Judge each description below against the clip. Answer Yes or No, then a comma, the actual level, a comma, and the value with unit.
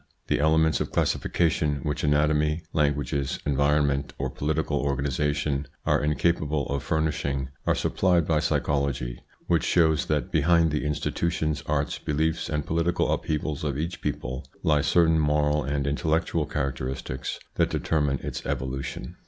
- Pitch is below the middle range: Yes, very low, 75 Hz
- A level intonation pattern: Yes, narrow, 2.0 semitones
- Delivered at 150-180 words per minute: No, slow, 135 wpm